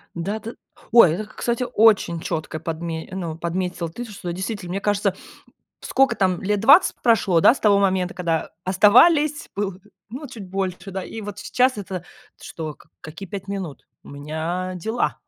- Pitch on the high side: Yes, high, 195 Hz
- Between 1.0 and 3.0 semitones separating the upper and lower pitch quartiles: No, average, 3.9 semitones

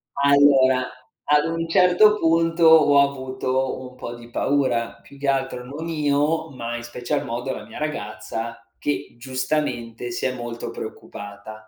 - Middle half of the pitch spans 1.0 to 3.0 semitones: No, average, 4.0 semitones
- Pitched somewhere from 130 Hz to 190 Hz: Yes, low, 135 Hz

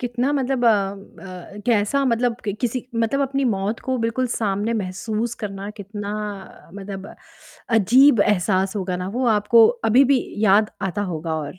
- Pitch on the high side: Yes, high, 210 Hz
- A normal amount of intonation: Yes, average, 3.7 semitones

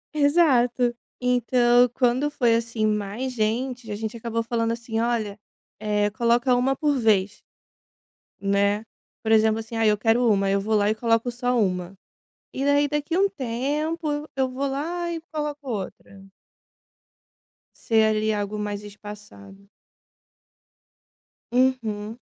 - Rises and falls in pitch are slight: No, average, 3.6 semitones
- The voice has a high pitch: Yes, high, 230 Hz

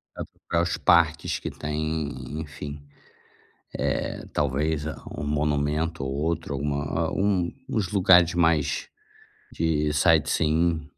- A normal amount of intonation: No, narrow, 2.3 semitones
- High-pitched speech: No, very low, 80 Hz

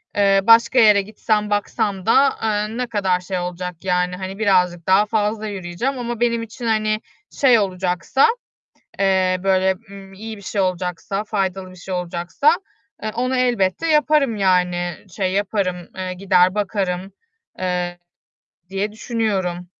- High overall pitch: Yes, high, 195 Hz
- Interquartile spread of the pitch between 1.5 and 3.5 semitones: Yes, average, 3.1 semitones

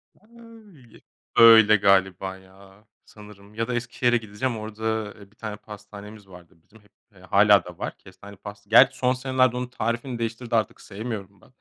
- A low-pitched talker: Yes, low, 110 Hz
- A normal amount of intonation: Yes, average, 3.1 semitones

